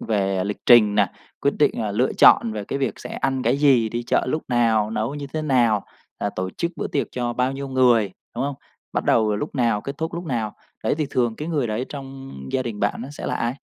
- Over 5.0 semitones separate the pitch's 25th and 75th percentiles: No, average, 4.0 semitones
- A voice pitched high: No, low, 120 Hz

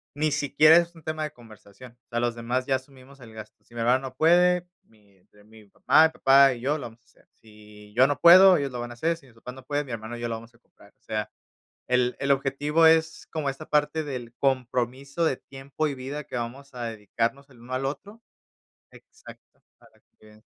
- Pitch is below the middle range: Yes, low, 130 Hz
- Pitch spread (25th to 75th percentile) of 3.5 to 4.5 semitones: Yes, average, 4.0 semitones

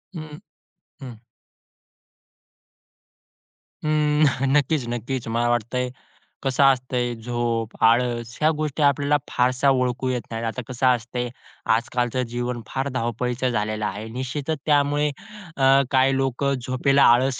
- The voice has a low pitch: Yes, low, 125 Hz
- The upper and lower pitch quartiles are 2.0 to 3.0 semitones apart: Yes, narrow, 2.6 semitones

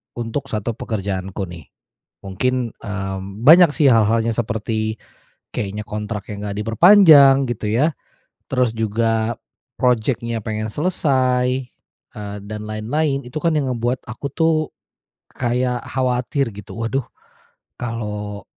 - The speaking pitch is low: Yes, low, 115 Hz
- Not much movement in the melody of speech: No, average, 3.5 semitones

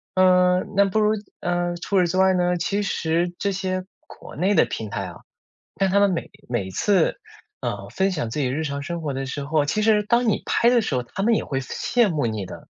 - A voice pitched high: No, medium, 180 Hz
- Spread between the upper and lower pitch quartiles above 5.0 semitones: Yes, wide, 5.6 semitones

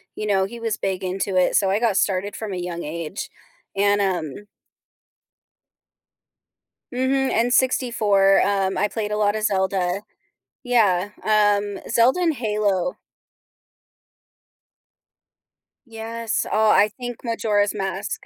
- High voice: Yes, high, 205 Hz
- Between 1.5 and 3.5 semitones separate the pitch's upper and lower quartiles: Yes, average, 2.8 semitones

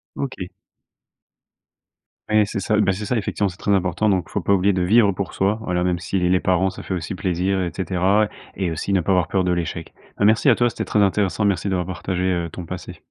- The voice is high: No, very low, 95 Hz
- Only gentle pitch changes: Yes, narrow, 2.1 semitones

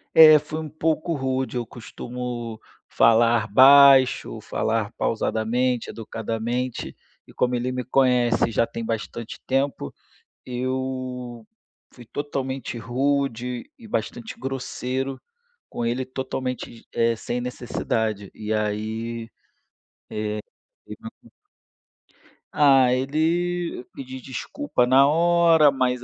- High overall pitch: No, low, 125 Hz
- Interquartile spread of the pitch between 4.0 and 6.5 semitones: No, average, 2.7 semitones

